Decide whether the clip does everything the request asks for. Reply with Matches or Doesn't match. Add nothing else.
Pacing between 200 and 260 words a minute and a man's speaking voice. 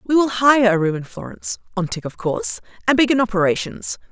Doesn't match